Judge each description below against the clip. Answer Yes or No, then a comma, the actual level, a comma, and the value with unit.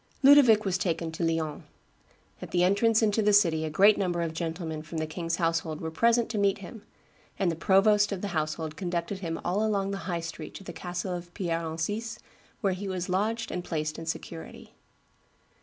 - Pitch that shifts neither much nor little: Yes, average, 3.6 semitones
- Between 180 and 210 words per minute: Yes, average, 200 wpm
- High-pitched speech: No, medium, 180 Hz